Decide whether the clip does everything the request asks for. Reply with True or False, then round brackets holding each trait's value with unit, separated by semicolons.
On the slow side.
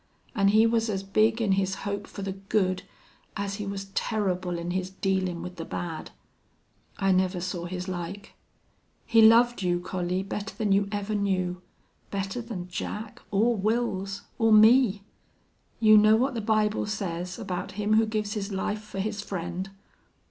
False (170 wpm)